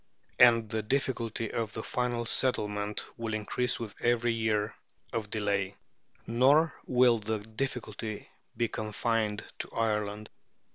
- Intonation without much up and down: Yes, narrow, 2.1 semitones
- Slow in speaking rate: Yes, slow, 125 wpm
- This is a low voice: Yes, low, 110 Hz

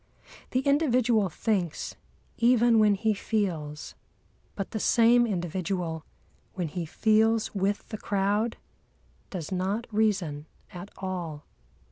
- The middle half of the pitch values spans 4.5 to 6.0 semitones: No, average, 3.9 semitones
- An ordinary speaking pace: No, slow, 110 wpm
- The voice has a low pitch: No, high, 200 Hz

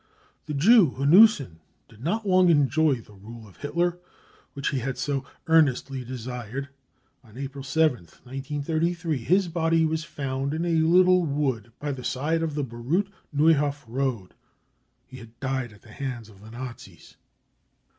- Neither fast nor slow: Yes, average, 155 wpm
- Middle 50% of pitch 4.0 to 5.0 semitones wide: Yes, average, 4.5 semitones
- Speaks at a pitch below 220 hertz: Yes, medium, 140 Hz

